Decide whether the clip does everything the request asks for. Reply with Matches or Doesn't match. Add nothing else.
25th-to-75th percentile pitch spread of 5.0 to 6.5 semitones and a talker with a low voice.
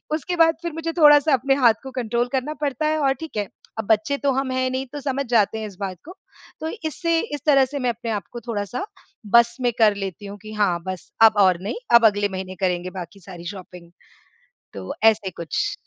Doesn't match